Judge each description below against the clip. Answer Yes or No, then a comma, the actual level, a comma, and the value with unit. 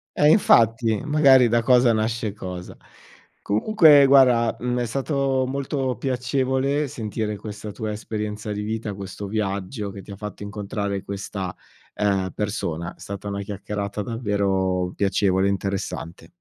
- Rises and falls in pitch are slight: No, average, 3.9 semitones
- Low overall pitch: Yes, low, 105 Hz